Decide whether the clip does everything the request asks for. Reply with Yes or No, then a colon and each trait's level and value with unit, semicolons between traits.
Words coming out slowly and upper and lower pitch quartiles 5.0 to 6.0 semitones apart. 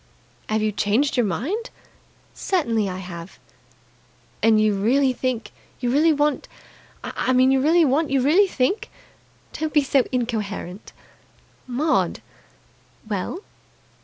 Yes: slow, 130 wpm; wide, 5.5 semitones